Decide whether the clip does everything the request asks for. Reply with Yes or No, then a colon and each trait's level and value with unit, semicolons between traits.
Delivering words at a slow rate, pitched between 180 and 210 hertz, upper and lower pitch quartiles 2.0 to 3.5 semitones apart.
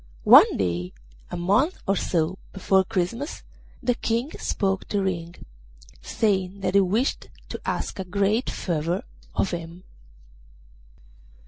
Yes: slow, 125 wpm; high, 190 Hz; average, 2.9 semitones